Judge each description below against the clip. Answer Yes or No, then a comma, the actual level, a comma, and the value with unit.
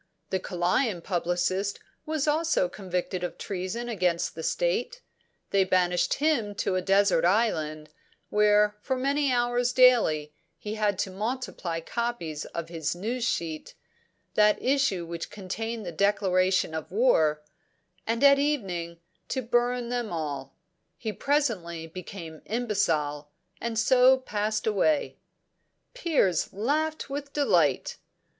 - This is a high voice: Yes, high, 205 Hz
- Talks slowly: Yes, slow, 125 wpm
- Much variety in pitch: Yes, wide, 6.0 semitones